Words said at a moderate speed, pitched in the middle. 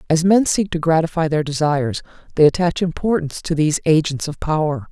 Yes: average, 185 wpm; medium, 160 Hz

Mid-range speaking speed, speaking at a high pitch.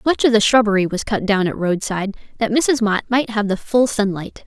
No: fast, 230 wpm; high, 215 Hz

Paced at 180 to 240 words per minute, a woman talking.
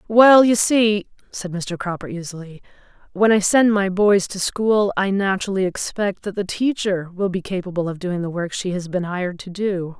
Yes: average, 200 wpm; female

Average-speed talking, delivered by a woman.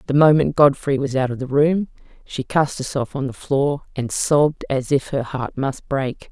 No: fast, 210 wpm; female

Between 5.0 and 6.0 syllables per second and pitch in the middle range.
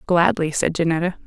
Yes: 5.6 syllables/s; medium, 170 Hz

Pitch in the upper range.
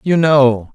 No: low, 135 Hz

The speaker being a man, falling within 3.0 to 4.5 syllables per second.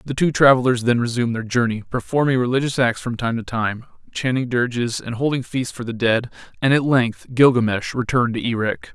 No: male; 5.8 syllables/s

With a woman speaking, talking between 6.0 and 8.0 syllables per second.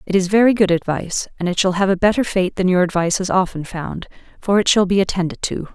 Yes: female; 6.4 syllables/s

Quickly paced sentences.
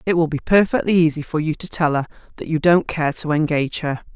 Yes: fast, 245 wpm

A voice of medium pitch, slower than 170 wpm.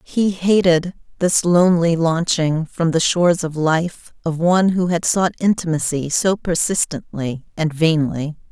Yes: medium, 170 Hz; average, 140 wpm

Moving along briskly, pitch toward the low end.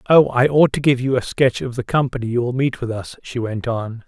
Yes: fast, 280 wpm; low, 125 Hz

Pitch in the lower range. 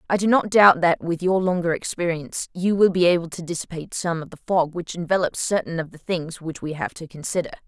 No: medium, 175 Hz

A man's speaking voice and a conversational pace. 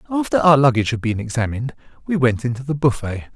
Yes: male; average, 195 wpm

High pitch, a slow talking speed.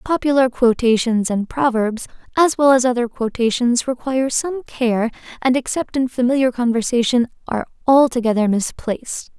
Yes: high, 245 Hz; slow, 130 wpm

